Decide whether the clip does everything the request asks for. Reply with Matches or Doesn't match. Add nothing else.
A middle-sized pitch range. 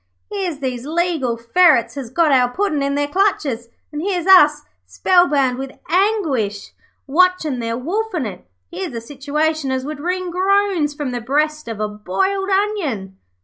Doesn't match